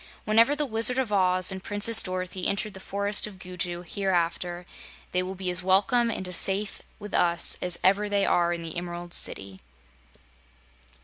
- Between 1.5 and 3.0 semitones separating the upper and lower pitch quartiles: Yes, narrow, 2.6 semitones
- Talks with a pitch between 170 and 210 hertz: Yes, high, 190 Hz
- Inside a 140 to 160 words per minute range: No, average, 175 wpm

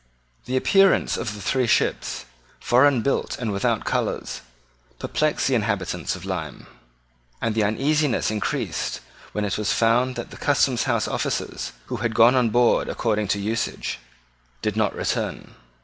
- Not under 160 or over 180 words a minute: No, average, 150 wpm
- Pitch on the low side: Yes, low, 115 Hz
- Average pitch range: Yes, average, 3.5 semitones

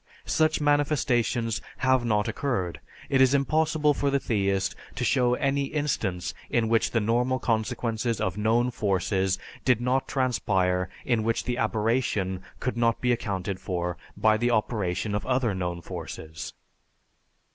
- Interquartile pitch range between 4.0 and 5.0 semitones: Yes, average, 4.6 semitones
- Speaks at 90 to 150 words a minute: Yes, average, 145 wpm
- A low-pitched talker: Yes, low, 115 Hz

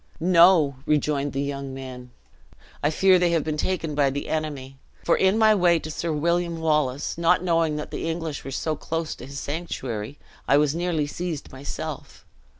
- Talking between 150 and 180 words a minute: Yes, average, 175 wpm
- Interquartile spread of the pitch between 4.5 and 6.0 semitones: No, average, 3.2 semitones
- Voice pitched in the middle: Yes, medium, 155 Hz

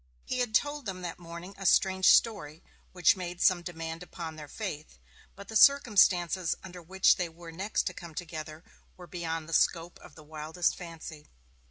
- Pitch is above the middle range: No, medium, 175 Hz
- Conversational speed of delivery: Yes, average, 180 wpm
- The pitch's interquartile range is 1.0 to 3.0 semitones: Yes, narrow, 2.6 semitones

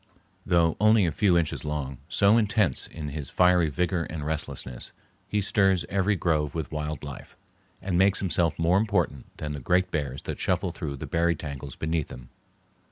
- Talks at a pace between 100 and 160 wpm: No, average, 175 wpm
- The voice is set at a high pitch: No, very low, 85 Hz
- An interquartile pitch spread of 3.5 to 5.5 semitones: Yes, average, 3.9 semitones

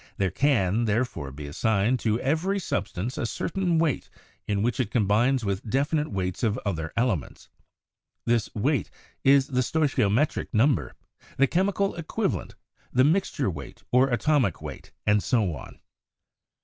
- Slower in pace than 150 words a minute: Yes, average, 140 wpm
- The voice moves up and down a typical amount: No, wide, 6.0 semitones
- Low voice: Yes, low, 120 Hz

